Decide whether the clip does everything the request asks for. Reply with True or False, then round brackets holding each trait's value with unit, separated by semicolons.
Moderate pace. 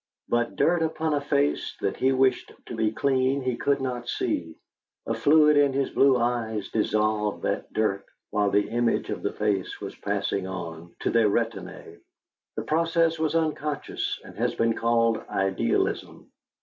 True (160 wpm)